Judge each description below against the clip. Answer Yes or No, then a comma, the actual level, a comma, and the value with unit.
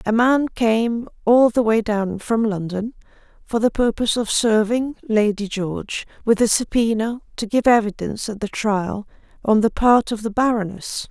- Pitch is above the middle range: Yes, high, 220 Hz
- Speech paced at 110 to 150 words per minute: No, average, 165 wpm